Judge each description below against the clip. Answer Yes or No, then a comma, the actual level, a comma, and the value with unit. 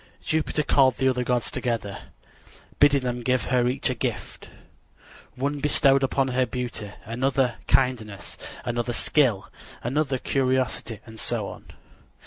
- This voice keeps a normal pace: No, slow, 130 wpm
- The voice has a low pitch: Yes, low, 125 Hz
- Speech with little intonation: Yes, narrow, 2.2 semitones